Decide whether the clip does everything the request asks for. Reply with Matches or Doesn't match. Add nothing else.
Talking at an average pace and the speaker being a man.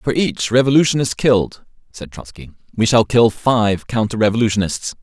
Matches